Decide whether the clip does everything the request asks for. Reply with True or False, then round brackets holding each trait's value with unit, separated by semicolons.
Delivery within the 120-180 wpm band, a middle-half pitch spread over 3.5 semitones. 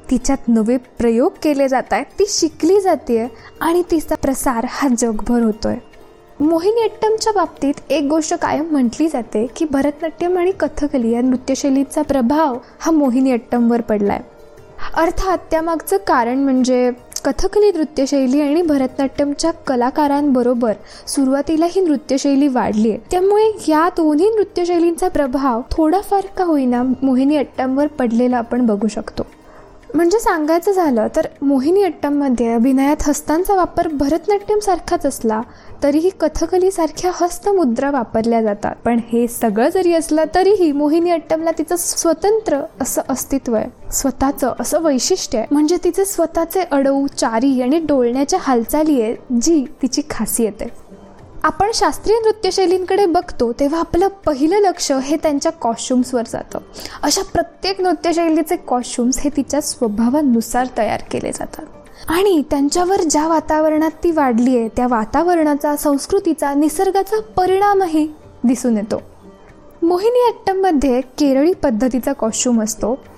True (125 wpm; 5.2 semitones)